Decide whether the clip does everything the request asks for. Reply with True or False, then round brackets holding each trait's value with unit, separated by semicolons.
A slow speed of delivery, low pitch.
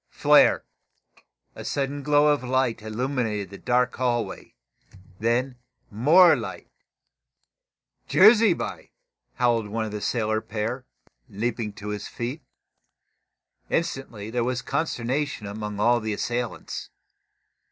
True (110 wpm; 120 Hz)